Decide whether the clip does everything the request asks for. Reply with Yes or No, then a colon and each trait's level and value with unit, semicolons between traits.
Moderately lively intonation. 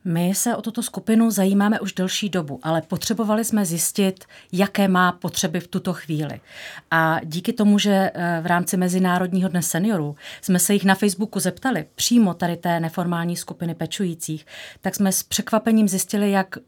Yes: average, 3.0 semitones